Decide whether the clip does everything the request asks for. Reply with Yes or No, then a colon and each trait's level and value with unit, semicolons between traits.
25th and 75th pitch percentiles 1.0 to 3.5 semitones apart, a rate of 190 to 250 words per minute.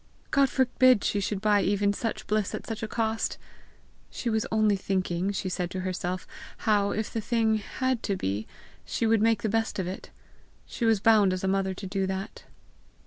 Yes: average, 2.8 semitones; average, 195 wpm